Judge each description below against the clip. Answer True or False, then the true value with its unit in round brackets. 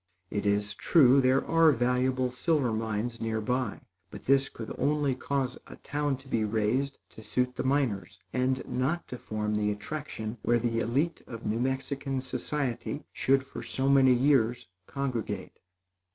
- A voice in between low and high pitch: False (125 Hz)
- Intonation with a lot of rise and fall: False (3.4 semitones)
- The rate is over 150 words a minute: True (160 wpm)